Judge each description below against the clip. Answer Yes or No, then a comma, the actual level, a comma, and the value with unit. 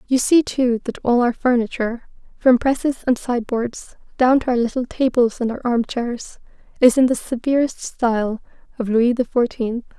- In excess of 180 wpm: No, average, 175 wpm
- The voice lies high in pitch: Yes, high, 245 Hz